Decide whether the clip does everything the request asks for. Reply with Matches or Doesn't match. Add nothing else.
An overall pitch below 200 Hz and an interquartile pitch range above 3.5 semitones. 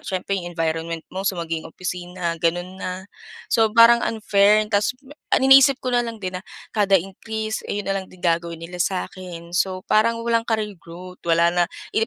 Matches